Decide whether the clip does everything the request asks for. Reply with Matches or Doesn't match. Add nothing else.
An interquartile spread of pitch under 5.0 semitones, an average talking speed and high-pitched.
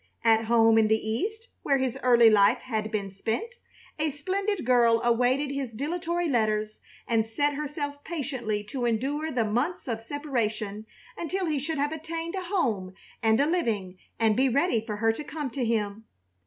Doesn't match